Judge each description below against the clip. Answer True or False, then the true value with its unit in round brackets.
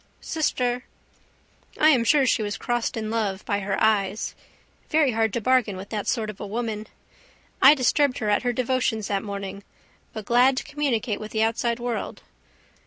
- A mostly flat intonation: False (3.3 semitones)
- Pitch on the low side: False (225 Hz)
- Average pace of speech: True (175 wpm)